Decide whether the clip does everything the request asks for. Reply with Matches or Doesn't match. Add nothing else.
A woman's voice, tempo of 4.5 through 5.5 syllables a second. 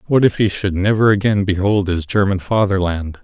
Doesn't match